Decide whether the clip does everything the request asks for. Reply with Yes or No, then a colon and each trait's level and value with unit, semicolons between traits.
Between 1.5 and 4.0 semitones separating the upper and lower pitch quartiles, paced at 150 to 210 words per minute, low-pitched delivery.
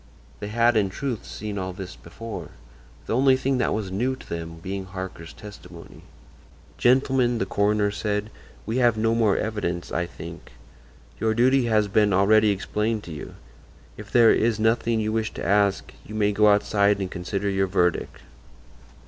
Yes: average, 2.8 semitones; average, 170 wpm; low, 105 Hz